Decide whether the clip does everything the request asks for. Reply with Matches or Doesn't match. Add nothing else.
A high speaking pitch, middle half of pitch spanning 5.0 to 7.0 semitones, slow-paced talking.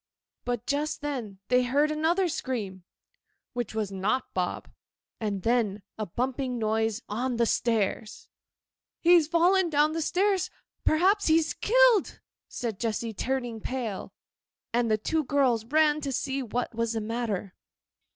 Matches